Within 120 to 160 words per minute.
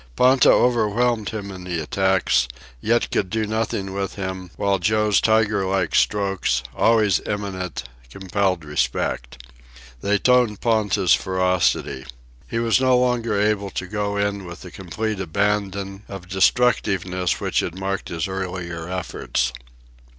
Yes: slow, 135 wpm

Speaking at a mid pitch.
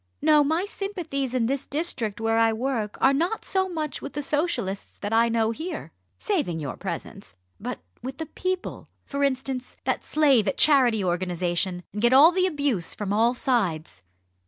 No: very high, 255 Hz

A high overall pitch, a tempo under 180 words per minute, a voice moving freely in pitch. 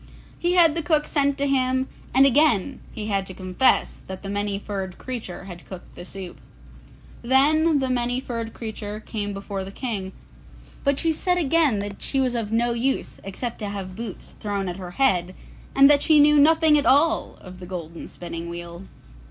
No: high, 230 Hz; average, 190 wpm; wide, 6.3 semitones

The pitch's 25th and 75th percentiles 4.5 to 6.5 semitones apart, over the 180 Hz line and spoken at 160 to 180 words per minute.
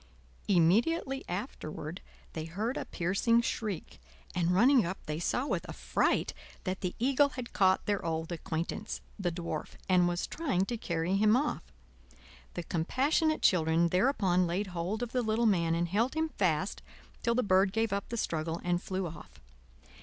Yes: wide, 5.4 semitones; high, 190 Hz; average, 165 wpm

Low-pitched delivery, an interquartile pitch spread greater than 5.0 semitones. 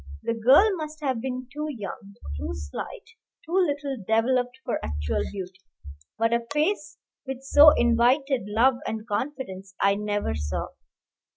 No: high, 235 Hz; wide, 5.5 semitones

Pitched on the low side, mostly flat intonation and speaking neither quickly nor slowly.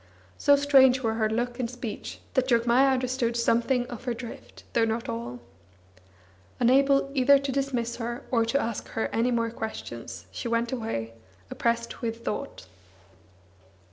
No: high, 235 Hz; narrow, 2.2 semitones; average, 150 wpm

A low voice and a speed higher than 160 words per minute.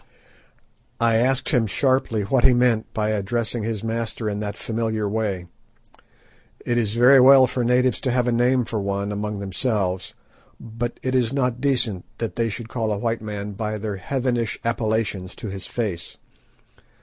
Yes: low, 115 Hz; average, 170 wpm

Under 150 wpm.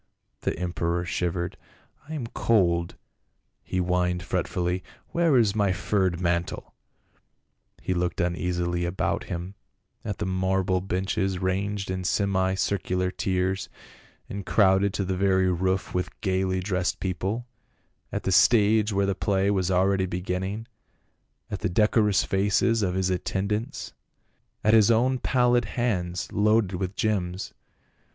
Yes: average, 140 wpm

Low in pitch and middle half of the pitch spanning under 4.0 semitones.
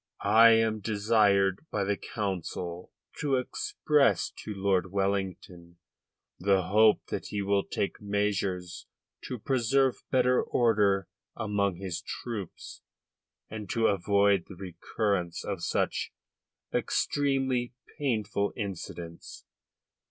Yes: low, 100 Hz; average, 2.9 semitones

